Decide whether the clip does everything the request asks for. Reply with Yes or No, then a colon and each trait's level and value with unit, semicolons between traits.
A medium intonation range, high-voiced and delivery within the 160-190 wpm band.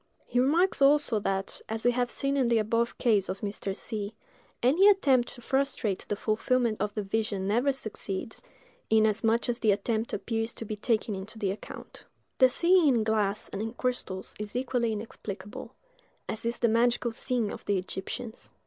Yes: average, 3.0 semitones; high, 225 Hz; average, 175 wpm